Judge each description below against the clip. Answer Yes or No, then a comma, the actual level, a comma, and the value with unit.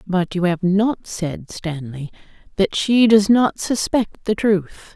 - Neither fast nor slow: Yes, average, 160 wpm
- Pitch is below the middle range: No, high, 195 Hz